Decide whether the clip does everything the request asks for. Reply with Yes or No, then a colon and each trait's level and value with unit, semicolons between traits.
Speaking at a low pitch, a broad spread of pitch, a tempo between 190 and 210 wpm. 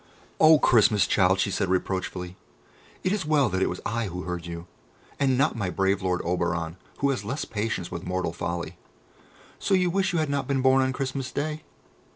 Yes: low, 105 Hz; wide, 7.4 semitones; average, 200 wpm